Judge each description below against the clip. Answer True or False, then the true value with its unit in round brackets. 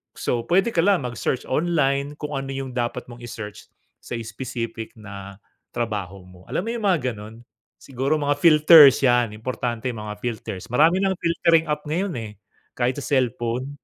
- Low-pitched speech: True (130 Hz)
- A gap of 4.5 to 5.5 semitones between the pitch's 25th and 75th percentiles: True (4.8 semitones)